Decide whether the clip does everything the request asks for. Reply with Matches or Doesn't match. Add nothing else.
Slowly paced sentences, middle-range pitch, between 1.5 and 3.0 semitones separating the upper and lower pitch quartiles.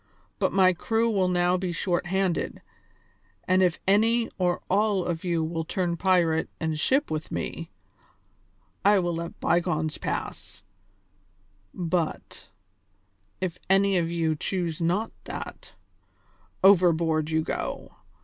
Matches